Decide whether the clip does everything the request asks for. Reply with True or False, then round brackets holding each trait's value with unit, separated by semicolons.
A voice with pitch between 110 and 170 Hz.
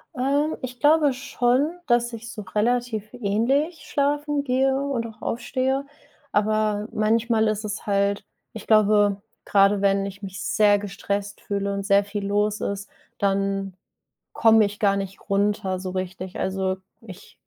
False (210 Hz)